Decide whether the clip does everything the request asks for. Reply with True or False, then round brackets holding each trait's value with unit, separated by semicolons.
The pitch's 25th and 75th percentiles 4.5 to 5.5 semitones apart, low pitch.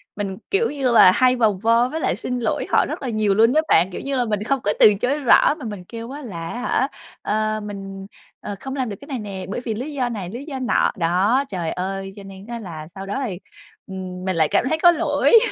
False (4.9 semitones; 215 Hz)